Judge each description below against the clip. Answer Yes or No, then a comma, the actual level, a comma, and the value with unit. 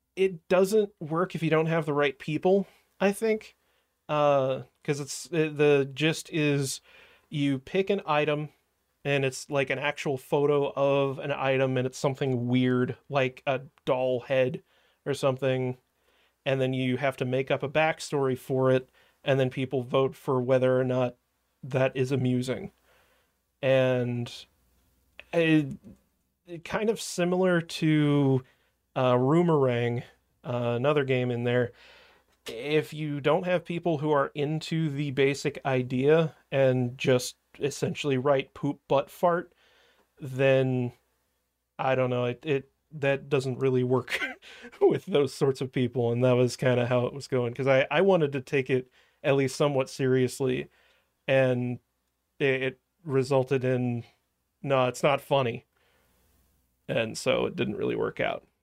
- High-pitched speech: No, low, 135 Hz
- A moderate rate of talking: Yes, average, 150 wpm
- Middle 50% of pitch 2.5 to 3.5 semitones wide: Yes, average, 2.8 semitones